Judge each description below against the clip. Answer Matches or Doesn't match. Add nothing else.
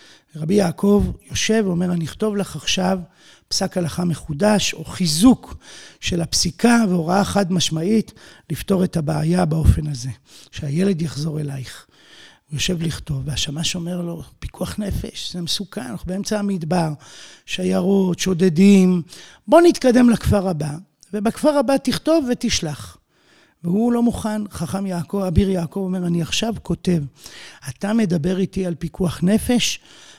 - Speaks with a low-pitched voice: Doesn't match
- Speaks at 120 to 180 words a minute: Matches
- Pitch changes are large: Doesn't match